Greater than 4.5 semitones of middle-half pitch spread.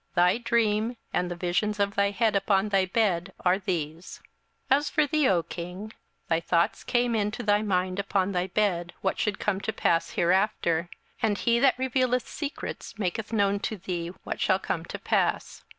No: average, 3.5 semitones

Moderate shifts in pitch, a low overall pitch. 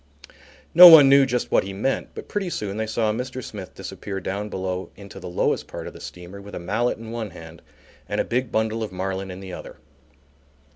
Yes: average, 3.9 semitones; low, 105 Hz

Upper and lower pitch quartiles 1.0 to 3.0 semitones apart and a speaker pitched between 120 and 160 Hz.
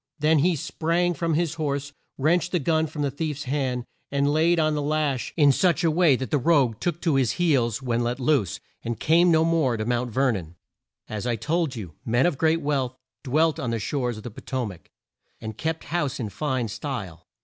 No: average, 4.7 semitones; medium, 140 Hz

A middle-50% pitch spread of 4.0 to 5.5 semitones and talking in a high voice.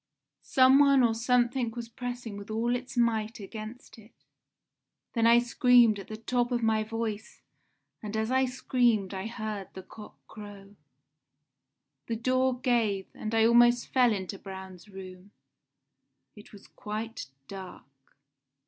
No: average, 2.7 semitones; high, 225 Hz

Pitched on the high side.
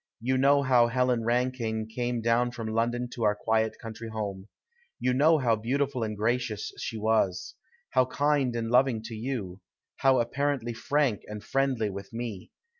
No: low, 120 Hz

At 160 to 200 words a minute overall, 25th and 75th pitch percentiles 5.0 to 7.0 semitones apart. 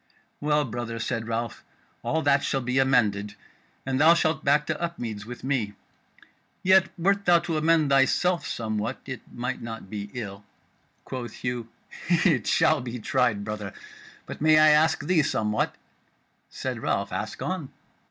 No: average, 150 wpm; wide, 5.6 semitones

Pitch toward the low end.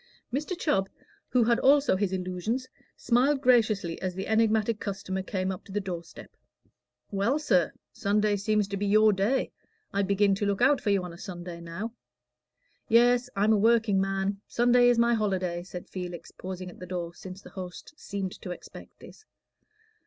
No: high, 200 Hz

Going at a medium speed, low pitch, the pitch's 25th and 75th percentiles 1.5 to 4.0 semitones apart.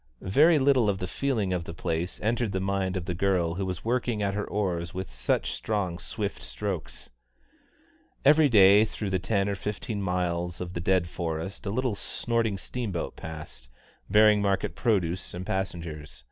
Yes: average, 175 wpm; very low, 95 Hz; average, 3.4 semitones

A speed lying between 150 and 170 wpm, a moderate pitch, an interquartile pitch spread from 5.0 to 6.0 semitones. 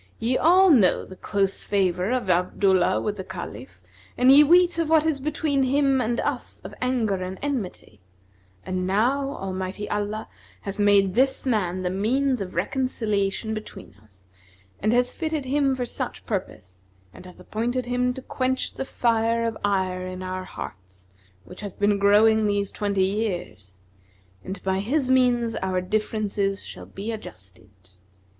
No: average, 160 wpm; high, 210 Hz; average, 5.3 semitones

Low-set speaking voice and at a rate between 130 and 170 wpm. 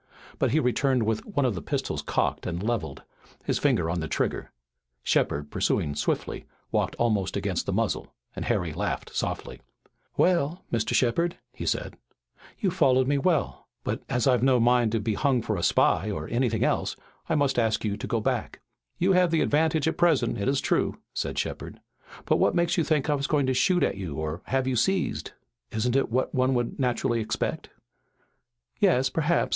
No: low, 125 Hz; average, 190 wpm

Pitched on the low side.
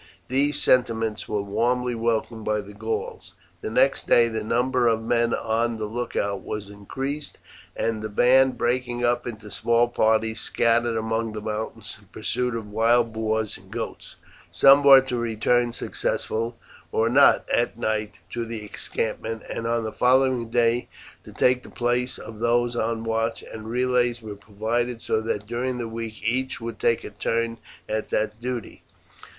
Yes: low, 115 Hz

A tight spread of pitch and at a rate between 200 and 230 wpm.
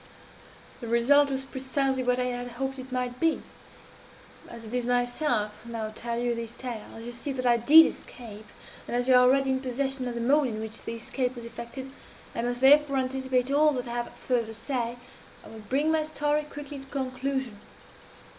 Yes: narrow, 2.3 semitones; fast, 205 wpm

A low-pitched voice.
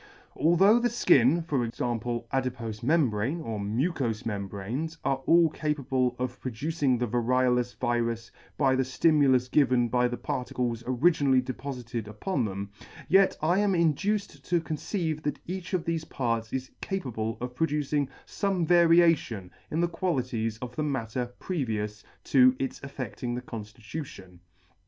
Yes: low, 130 Hz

